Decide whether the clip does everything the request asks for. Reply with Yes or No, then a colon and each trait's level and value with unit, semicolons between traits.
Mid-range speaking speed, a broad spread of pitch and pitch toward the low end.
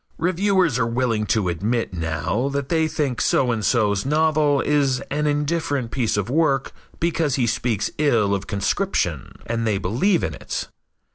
Yes: average, 160 wpm; wide, 5.9 semitones; low, 130 Hz